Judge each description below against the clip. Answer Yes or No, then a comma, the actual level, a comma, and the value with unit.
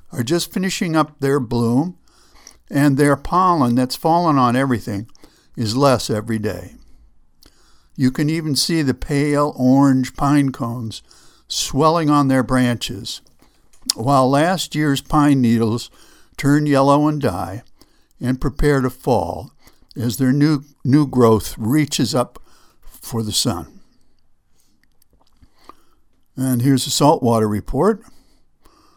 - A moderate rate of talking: No, slow, 120 wpm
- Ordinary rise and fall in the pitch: Yes, average, 3.5 semitones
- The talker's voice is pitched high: No, low, 135 Hz